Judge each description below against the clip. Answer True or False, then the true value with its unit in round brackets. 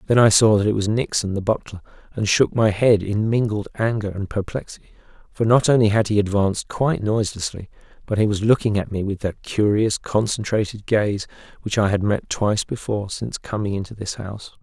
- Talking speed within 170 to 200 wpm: True (195 wpm)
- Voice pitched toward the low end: True (105 Hz)